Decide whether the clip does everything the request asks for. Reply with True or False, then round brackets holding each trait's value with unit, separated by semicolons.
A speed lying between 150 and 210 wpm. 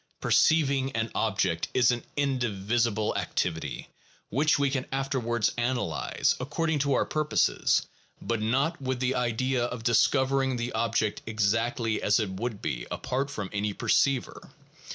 False (135 wpm)